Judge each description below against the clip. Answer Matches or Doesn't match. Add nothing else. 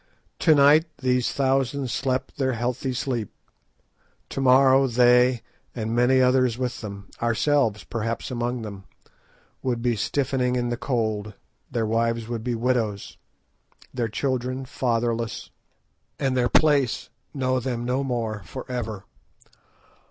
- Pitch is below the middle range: Matches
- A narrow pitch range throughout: Matches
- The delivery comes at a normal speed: Doesn't match